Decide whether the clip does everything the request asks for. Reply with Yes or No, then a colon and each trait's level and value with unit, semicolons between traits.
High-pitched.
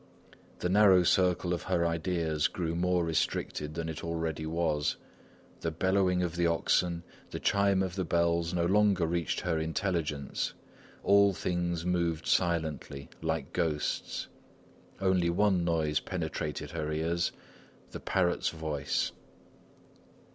No: very low, 85 Hz